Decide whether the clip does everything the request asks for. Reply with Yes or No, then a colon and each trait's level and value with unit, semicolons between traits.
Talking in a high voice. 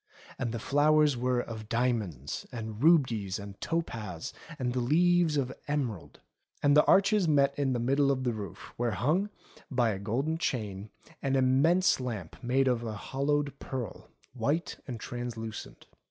No: low, 125 Hz